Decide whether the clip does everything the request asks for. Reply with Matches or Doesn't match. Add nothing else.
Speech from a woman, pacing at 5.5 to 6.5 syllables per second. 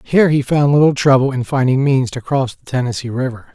Doesn't match